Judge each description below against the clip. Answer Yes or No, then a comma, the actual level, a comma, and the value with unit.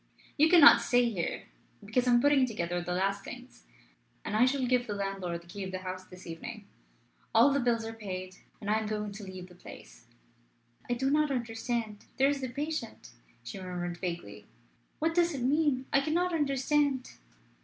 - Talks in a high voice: Yes, high, 225 Hz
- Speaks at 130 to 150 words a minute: No, average, 190 wpm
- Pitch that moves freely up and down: Yes, wide, 6.5 semitones